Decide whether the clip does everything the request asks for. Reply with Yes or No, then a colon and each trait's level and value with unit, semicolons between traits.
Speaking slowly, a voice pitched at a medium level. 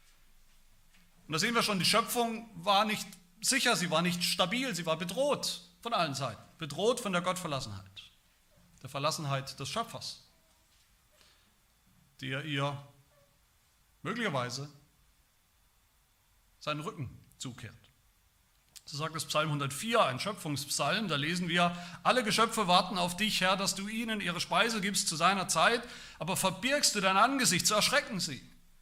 No: average, 140 wpm; medium, 175 Hz